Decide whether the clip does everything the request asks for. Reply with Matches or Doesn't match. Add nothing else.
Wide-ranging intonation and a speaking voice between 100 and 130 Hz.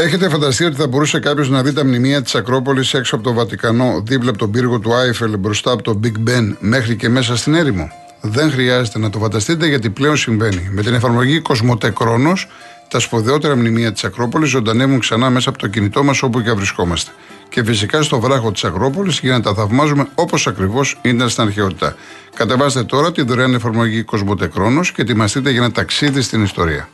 Doesn't match